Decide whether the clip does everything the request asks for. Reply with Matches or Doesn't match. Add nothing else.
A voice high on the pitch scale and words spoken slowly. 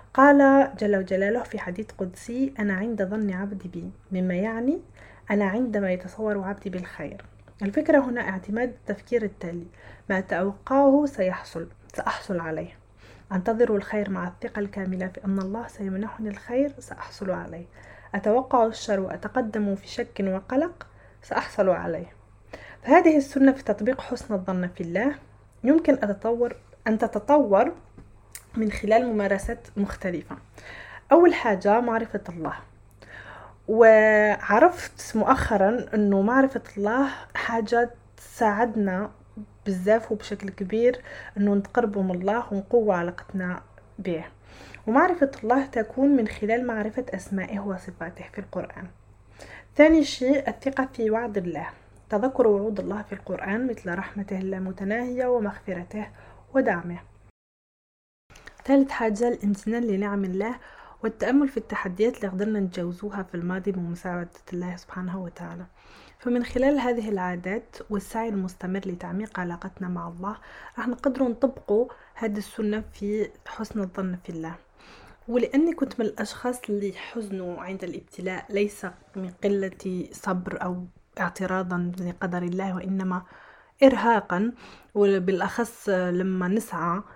Matches